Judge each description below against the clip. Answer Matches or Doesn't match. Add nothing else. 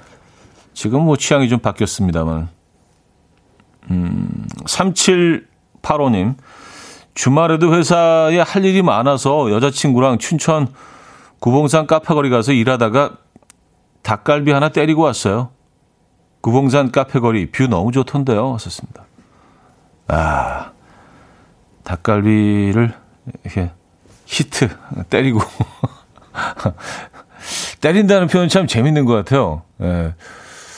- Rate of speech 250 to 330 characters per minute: Doesn't match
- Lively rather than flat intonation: Matches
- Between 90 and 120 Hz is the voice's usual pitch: Doesn't match